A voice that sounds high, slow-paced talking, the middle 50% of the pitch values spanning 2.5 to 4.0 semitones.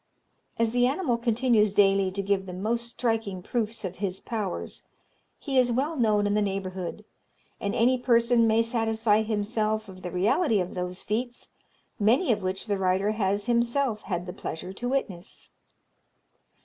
No: high, 215 Hz; average, 160 wpm; average, 3.5 semitones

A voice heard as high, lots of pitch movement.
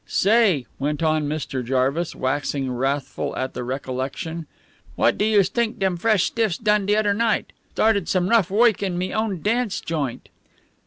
No: medium, 180 Hz; wide, 6.9 semitones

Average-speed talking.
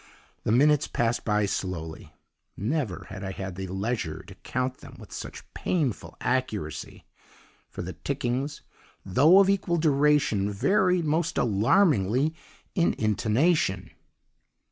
No: slow, 120 wpm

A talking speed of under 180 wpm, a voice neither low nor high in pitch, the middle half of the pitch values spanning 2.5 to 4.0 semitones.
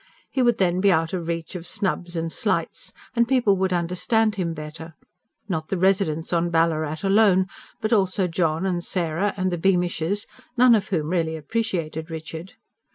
Yes: average, 170 wpm; medium, 175 Hz; average, 3.2 semitones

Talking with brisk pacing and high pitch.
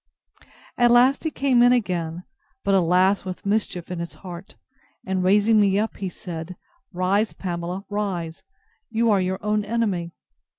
No: average, 155 wpm; high, 195 Hz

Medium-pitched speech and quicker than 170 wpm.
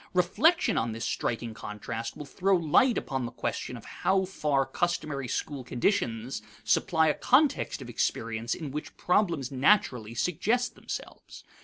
No: medium, 145 Hz; average, 145 wpm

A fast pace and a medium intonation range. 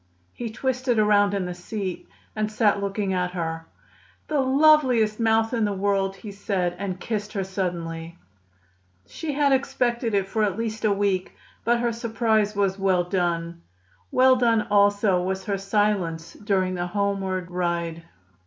No: average, 160 wpm; average, 3.3 semitones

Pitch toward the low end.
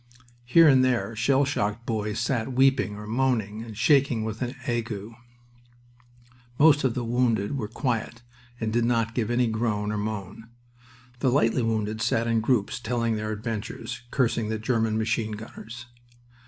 Yes: low, 115 Hz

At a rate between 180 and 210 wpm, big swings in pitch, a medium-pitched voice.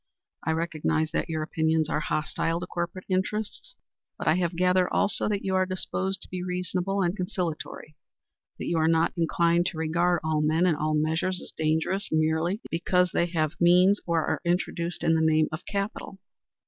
No: average, 185 wpm; narrow, 2.4 semitones; medium, 170 Hz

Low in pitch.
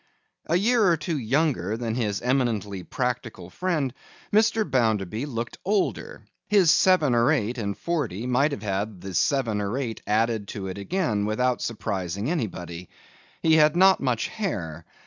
Yes: low, 120 Hz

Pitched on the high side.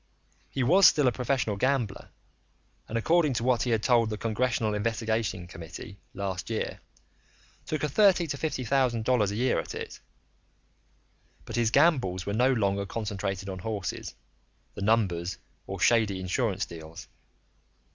No: low, 115 Hz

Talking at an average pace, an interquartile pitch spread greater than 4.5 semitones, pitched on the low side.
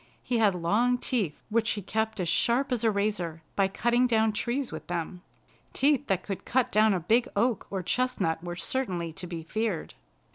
No: average, 190 wpm; average, 5.1 semitones; high, 210 Hz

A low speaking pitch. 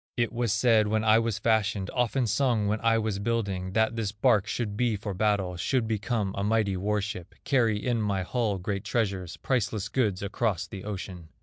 Yes: low, 105 Hz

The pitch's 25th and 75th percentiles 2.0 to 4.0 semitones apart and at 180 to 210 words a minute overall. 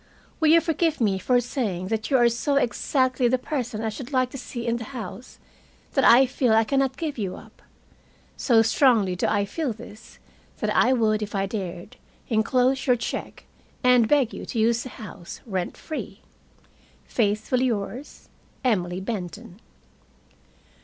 No: average, 3.4 semitones; average, 165 wpm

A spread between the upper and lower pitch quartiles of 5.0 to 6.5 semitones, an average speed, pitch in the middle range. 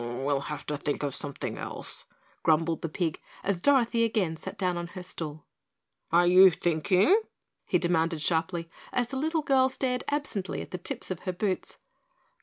Yes: wide, 5.6 semitones; average, 175 wpm; medium, 180 Hz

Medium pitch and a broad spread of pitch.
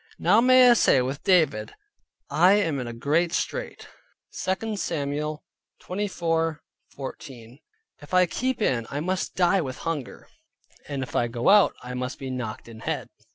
Yes: medium, 155 Hz; wide, 6.5 semitones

